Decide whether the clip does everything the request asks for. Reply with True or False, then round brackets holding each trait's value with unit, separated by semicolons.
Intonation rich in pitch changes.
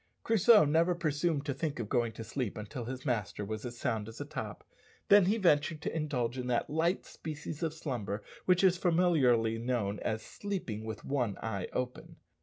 True (6.5 semitones)